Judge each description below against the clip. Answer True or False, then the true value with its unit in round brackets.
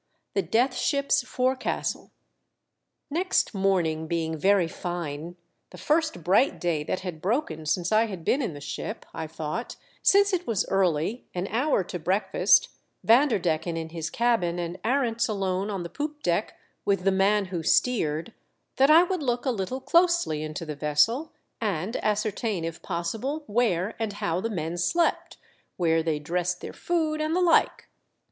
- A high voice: True (195 Hz)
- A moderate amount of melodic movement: False (6.9 semitones)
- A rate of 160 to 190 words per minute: True (170 wpm)